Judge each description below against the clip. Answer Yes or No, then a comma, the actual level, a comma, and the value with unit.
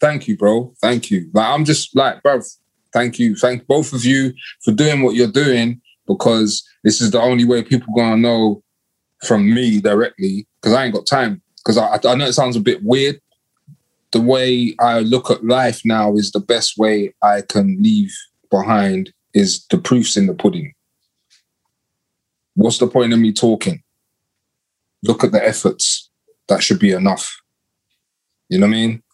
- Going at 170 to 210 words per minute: Yes, average, 180 wpm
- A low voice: Yes, low, 120 Hz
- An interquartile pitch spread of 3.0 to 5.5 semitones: Yes, average, 4.0 semitones